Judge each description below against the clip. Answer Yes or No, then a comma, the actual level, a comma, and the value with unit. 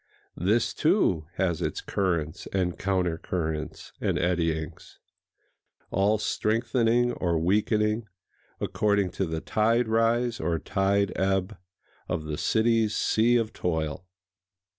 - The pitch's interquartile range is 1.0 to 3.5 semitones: No, average, 4.5 semitones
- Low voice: Yes, very low, 95 Hz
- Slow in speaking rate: Yes, slow, 120 wpm